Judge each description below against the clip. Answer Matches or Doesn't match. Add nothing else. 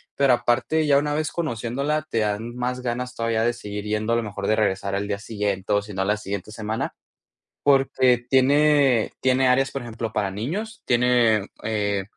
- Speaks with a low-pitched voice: Matches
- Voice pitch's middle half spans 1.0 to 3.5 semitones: Doesn't match